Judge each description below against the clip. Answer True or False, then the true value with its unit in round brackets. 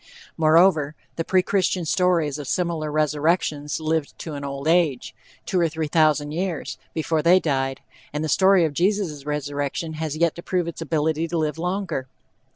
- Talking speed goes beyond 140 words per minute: True (170 wpm)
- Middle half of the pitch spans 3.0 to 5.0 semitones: False (2.5 semitones)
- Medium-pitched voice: True (160 Hz)